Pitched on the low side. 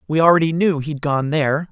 No: medium, 155 Hz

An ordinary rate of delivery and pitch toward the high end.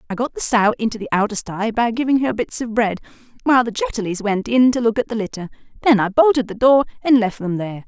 No: fast, 250 wpm; high, 225 Hz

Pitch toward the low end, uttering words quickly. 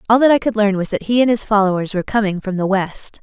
No: high, 210 Hz; fast, 295 wpm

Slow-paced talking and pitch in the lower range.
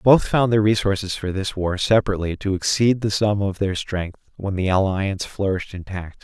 No: average, 190 wpm; low, 100 Hz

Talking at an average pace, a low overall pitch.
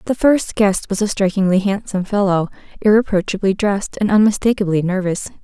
No: average, 145 wpm; high, 200 Hz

